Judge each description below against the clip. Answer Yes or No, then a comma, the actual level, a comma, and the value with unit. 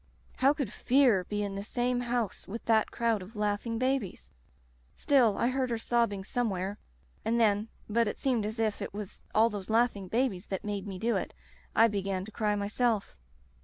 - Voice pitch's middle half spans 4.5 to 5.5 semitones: No, average, 2.9 semitones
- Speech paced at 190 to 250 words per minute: Yes, average, 200 wpm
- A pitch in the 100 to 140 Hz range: No, high, 220 Hz